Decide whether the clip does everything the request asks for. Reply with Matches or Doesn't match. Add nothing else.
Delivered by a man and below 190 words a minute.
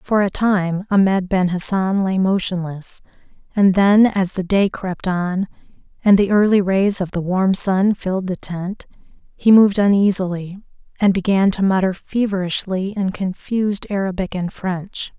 Doesn't match